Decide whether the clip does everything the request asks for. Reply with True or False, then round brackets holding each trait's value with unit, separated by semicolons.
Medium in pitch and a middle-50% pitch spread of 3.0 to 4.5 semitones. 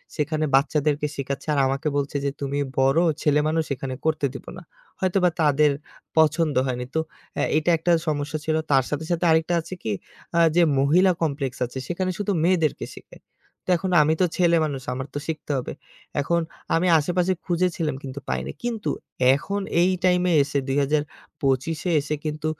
True (155 Hz; 3.5 semitones)